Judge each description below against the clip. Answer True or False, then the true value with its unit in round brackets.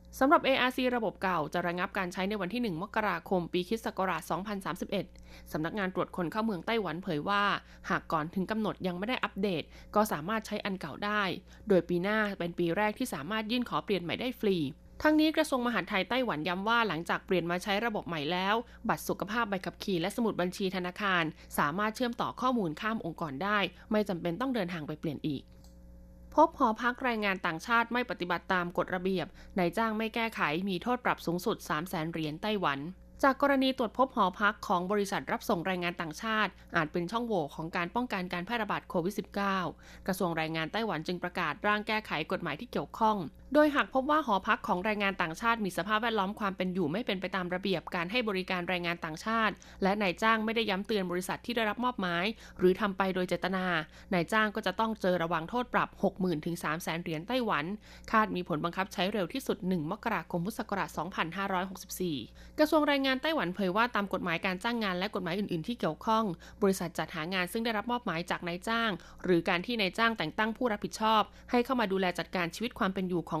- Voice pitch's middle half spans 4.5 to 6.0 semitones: False (4.1 semitones)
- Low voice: False (195 Hz)